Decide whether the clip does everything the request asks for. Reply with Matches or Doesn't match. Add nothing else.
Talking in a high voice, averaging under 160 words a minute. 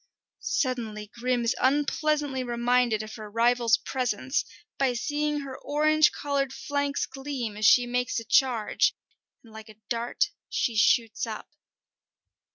Matches